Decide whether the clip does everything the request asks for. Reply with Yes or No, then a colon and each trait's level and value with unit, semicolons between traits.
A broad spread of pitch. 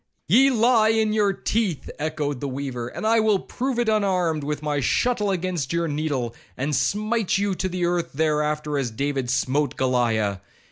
Yes: wide, 7.0 semitones